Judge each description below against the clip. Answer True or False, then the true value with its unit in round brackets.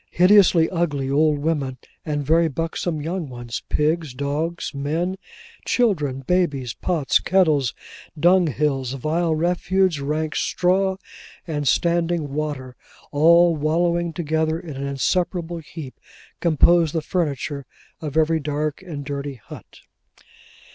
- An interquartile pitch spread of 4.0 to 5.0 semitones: False (3.2 semitones)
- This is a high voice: False (155 Hz)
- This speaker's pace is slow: True (120 wpm)